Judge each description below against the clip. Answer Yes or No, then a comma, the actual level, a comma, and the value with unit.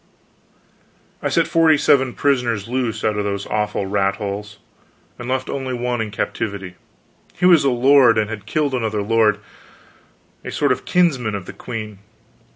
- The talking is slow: No, average, 160 wpm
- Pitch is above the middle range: No, low, 115 Hz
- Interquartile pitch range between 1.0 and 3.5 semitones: No, average, 3.9 semitones